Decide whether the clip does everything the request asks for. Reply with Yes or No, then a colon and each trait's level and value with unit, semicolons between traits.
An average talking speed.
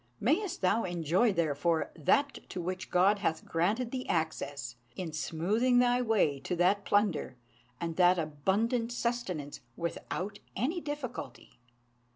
No: slow, 130 wpm